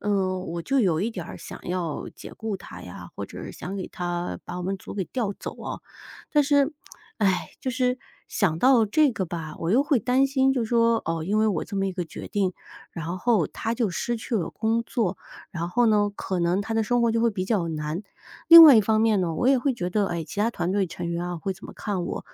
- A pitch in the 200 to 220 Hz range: Yes, high, 205 Hz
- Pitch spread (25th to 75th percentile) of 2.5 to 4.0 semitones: No, average, 4.7 semitones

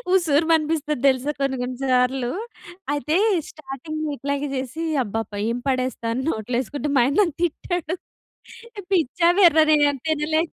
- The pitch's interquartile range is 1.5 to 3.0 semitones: No, average, 3.5 semitones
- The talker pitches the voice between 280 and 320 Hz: Yes, very high, 290 Hz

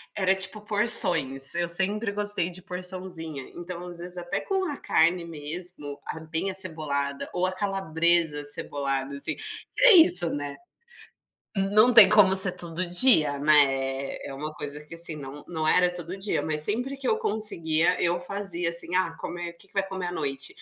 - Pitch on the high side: No, medium, 175 Hz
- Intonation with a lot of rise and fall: No, average, 3.6 semitones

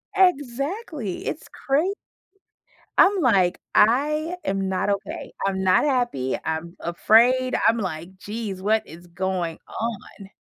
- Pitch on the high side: Yes, high, 215 Hz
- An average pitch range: No, wide, 6.6 semitones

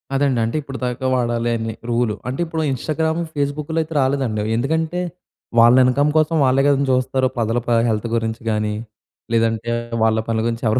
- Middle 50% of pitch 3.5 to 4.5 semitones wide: Yes, average, 3.8 semitones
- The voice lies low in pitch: Yes, low, 125 Hz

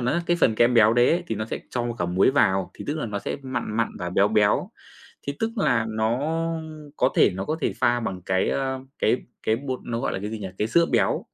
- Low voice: Yes, low, 115 Hz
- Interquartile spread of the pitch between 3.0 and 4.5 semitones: Yes, average, 3.8 semitones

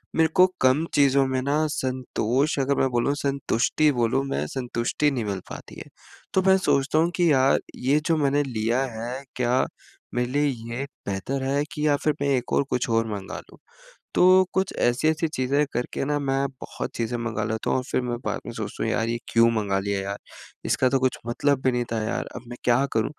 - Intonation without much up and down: No, average, 3.4 semitones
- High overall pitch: No, low, 130 Hz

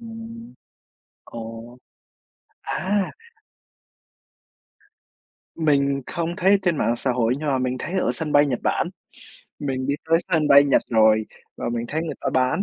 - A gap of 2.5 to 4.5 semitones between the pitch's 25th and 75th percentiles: No, average, 5.2 semitones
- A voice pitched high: No, medium, 140 Hz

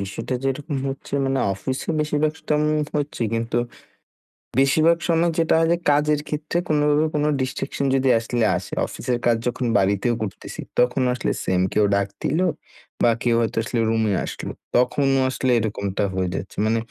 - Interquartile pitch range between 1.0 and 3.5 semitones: No, average, 4.6 semitones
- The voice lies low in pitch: Yes, low, 130 Hz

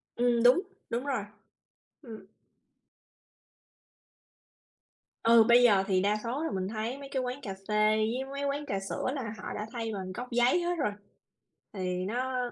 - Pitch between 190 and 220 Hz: No, high, 235 Hz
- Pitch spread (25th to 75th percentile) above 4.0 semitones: No, average, 3.4 semitones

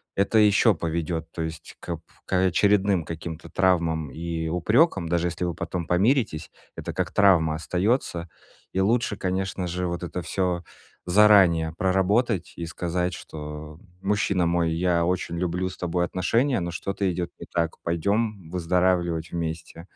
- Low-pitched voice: Yes, very low, 90 Hz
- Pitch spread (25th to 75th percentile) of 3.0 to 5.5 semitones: No, narrow, 2.4 semitones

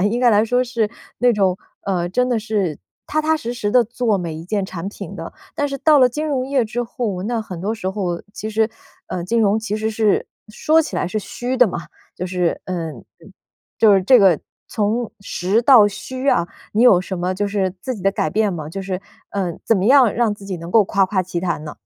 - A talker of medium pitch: No, high, 210 Hz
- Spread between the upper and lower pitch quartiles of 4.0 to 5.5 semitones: Yes, average, 4.4 semitones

